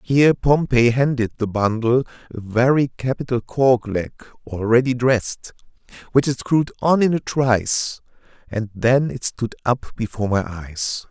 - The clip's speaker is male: Yes, male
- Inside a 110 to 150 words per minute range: Yes, average, 145 wpm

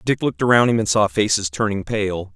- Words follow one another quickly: Yes, fast, 230 wpm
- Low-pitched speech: Yes, low, 105 Hz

